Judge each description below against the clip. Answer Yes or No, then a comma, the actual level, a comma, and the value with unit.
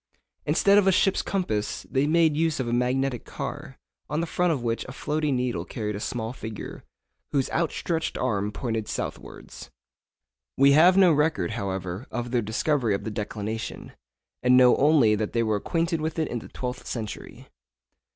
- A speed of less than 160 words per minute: No, average, 175 wpm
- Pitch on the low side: Yes, low, 125 Hz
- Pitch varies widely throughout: Yes, wide, 5.9 semitones